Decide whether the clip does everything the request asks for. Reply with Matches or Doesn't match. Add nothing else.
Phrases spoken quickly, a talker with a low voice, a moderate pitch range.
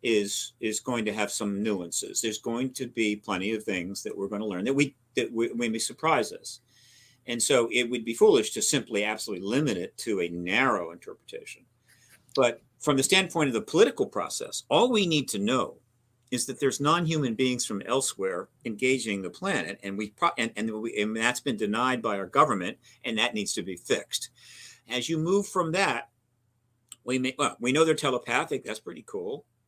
Matches